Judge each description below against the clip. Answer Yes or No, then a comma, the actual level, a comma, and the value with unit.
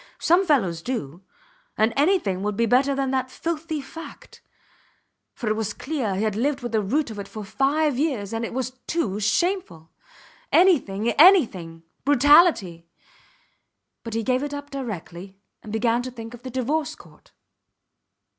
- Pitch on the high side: Yes, high, 245 Hz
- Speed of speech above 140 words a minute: Yes, average, 160 wpm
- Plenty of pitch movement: Yes, wide, 5.7 semitones